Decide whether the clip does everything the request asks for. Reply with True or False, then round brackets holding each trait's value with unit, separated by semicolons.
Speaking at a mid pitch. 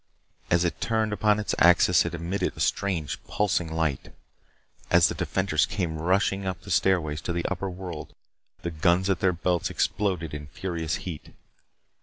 False (90 Hz)